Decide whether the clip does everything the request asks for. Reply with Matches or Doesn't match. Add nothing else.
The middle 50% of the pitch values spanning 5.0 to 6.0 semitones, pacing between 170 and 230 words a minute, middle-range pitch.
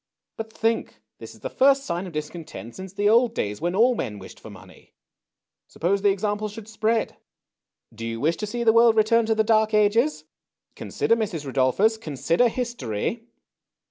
Doesn't match